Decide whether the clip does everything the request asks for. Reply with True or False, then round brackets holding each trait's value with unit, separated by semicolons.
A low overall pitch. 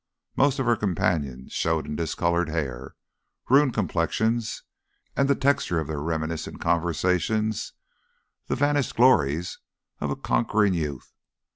True (85 Hz)